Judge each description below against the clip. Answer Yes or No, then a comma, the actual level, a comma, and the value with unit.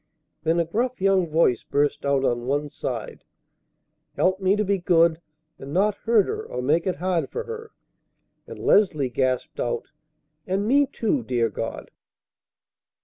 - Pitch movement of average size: No, wide, 6.3 semitones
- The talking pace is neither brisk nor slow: Yes, average, 155 wpm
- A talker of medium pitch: Yes, medium, 170 Hz